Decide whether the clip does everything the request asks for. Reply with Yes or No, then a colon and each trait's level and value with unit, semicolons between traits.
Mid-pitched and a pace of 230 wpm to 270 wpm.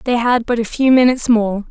No: high, 235 Hz; fast, 245 wpm